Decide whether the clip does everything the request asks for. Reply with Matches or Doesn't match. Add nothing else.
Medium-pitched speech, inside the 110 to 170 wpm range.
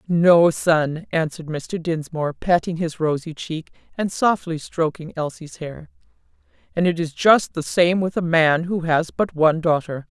Matches